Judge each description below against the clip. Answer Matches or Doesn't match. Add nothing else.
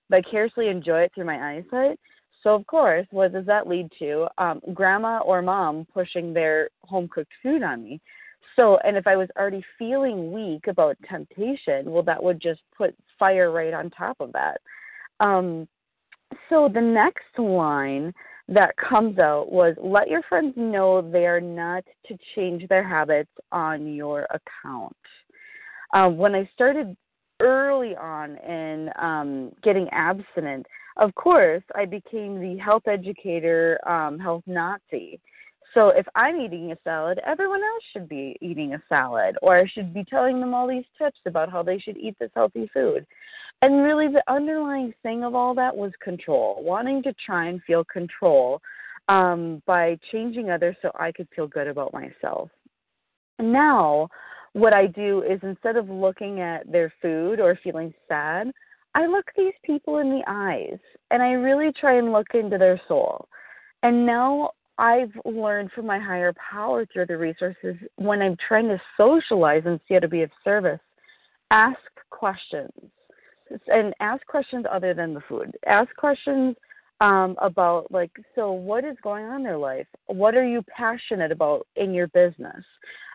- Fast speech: Doesn't match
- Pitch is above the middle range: Matches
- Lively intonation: Matches